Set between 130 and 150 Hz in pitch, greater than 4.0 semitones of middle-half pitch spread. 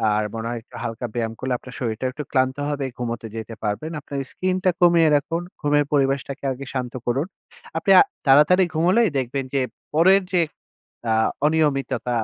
Yes: low, 135 Hz; average, 4.6 semitones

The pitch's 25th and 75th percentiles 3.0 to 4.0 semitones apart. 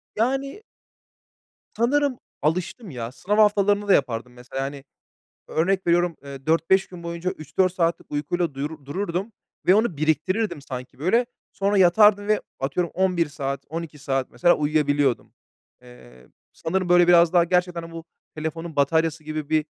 No: average, 4.6 semitones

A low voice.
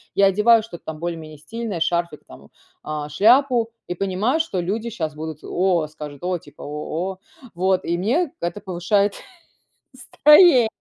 No: medium, 185 Hz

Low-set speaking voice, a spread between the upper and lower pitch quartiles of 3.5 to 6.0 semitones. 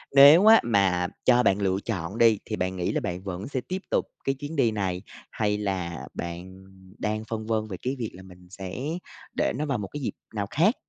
Yes: low, 105 Hz; average, 4.9 semitones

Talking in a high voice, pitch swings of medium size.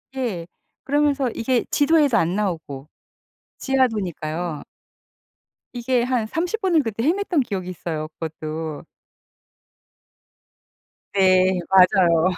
No: high, 205 Hz; wide, 7.8 semitones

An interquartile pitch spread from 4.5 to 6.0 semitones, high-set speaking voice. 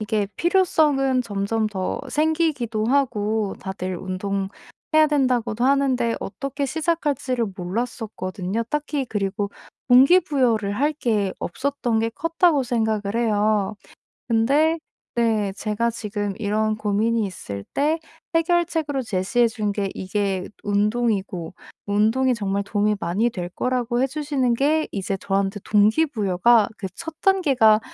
Yes: average, 5.1 semitones; high, 225 Hz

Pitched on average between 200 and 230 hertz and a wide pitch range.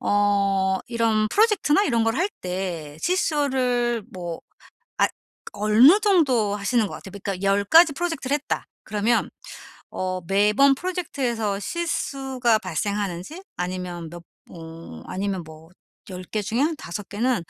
Yes: high, 210 Hz; wide, 6.1 semitones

